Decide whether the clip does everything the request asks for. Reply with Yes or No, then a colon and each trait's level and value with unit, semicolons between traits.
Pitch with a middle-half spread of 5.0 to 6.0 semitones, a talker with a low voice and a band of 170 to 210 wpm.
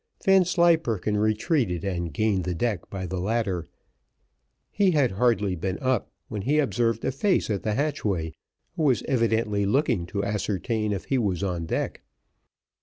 No: wide, 5.4 semitones; low, 105 Hz; average, 155 wpm